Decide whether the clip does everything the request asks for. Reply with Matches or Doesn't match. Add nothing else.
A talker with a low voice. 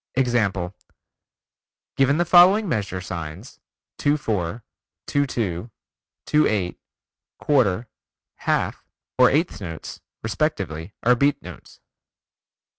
Matches